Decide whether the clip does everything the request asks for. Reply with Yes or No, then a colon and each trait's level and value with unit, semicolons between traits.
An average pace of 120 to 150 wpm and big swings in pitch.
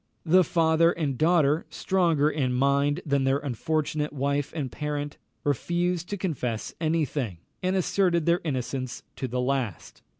No: average, 145 wpm; average, 3.7 semitones